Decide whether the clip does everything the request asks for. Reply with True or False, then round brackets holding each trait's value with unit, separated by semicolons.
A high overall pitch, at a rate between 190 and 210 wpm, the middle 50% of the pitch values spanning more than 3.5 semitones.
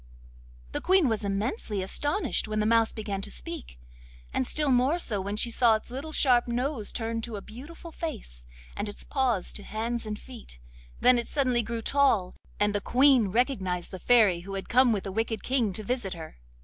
True (225 Hz; 200 wpm; 4.1 semitones)